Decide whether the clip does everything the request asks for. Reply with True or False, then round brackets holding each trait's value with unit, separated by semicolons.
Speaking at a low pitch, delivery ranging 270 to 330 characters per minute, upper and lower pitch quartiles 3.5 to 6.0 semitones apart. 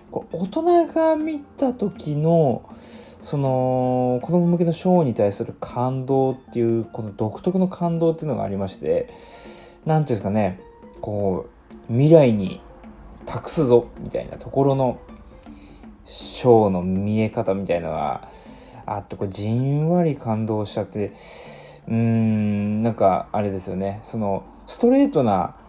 False (120 Hz; 280 characters per minute; 7.7 semitones)